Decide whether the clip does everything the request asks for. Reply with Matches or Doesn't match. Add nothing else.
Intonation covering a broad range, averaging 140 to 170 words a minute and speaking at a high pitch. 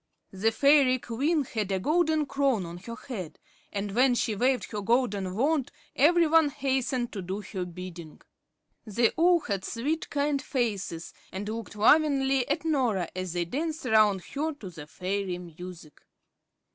Matches